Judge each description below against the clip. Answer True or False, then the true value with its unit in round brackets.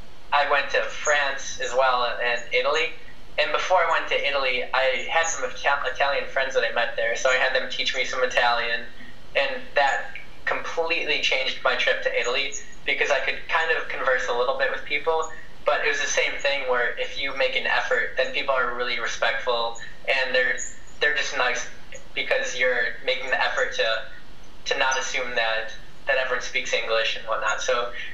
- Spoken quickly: False (190 wpm)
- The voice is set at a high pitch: True (300 Hz)